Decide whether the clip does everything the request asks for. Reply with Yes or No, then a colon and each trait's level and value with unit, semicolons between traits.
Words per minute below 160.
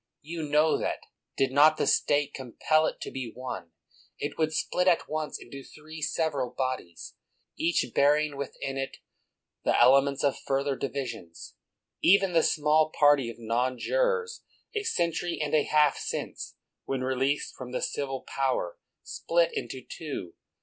Yes: average, 150 wpm